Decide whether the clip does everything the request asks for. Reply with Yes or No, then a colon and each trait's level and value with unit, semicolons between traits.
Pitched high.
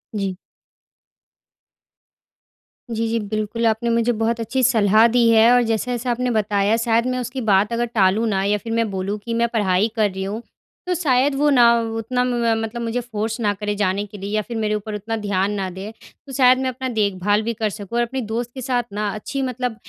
Yes: high, 225 Hz